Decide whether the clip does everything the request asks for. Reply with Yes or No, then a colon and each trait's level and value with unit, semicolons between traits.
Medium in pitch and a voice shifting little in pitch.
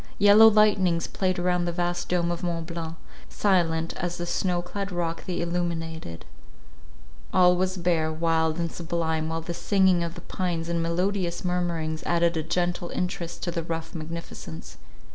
Yes: medium, 170 Hz; narrow, 1.4 semitones